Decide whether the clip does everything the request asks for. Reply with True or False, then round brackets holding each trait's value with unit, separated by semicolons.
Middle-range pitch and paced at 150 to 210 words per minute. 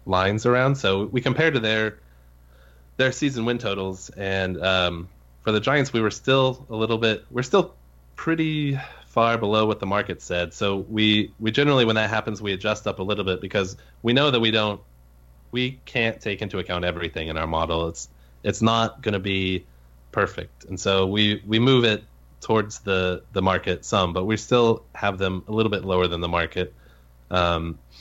False (100 Hz; 195 wpm)